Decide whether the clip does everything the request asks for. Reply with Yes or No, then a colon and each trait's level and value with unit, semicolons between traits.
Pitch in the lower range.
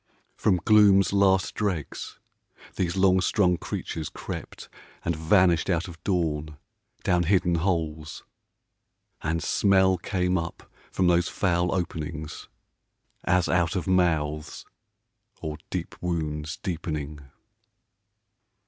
Yes: very low, 85 Hz